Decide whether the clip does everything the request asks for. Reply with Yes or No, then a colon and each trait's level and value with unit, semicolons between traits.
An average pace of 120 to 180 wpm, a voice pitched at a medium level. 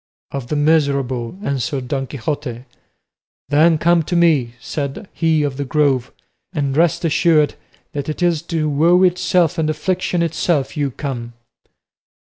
Yes: average, 140 wpm; medium, 150 Hz